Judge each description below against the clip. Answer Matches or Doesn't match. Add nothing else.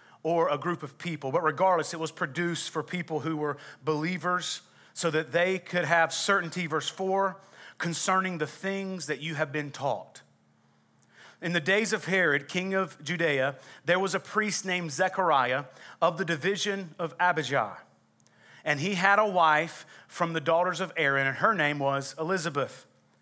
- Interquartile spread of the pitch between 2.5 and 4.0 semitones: Matches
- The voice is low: Doesn't match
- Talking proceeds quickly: Doesn't match